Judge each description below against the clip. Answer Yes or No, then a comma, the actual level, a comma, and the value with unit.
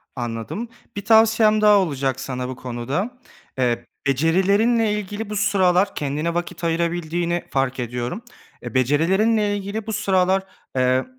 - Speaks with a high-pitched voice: No, medium, 175 Hz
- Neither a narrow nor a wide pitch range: No, wide, 7.6 semitones